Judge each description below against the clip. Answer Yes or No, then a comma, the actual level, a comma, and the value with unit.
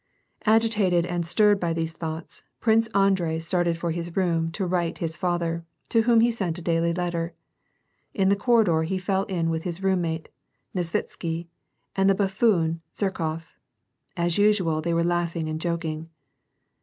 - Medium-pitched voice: Yes, medium, 175 Hz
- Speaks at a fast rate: No, average, 155 wpm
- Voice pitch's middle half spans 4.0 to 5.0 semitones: No, average, 2.7 semitones